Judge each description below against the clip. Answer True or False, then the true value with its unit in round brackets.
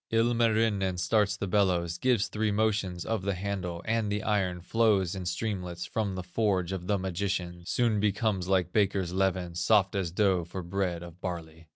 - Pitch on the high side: False (95 Hz)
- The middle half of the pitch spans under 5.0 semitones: True (2.9 semitones)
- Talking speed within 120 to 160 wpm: False (175 wpm)